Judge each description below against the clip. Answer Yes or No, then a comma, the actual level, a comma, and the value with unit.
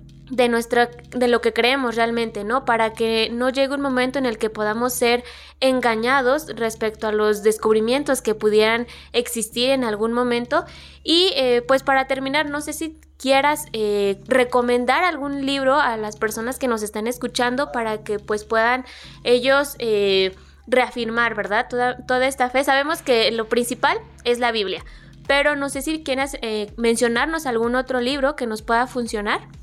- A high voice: Yes, high, 245 Hz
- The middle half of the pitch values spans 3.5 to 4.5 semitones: No, average, 2.9 semitones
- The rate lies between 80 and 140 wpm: No, average, 170 wpm